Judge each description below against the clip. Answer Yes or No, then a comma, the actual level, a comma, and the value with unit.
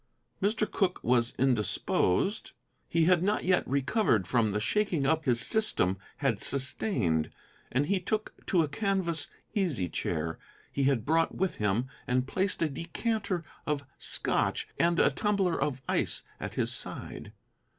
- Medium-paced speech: Yes, average, 150 wpm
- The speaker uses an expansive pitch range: Yes, wide, 7.8 semitones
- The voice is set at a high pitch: No, medium, 150 Hz